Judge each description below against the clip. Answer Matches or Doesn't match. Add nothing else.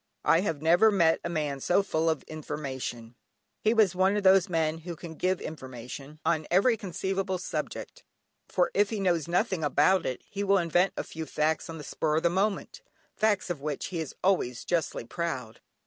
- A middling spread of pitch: Matches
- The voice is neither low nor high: Matches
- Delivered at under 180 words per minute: Doesn't match